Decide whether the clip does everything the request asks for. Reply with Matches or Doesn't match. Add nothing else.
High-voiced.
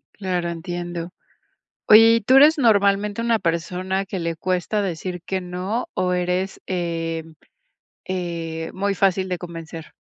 Doesn't match